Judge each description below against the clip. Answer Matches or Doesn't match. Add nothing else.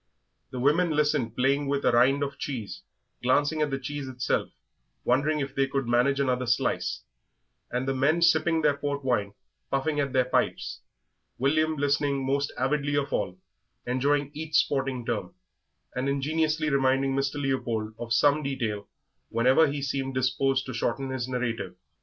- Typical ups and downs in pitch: Doesn't match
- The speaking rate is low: Doesn't match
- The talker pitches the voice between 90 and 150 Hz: Matches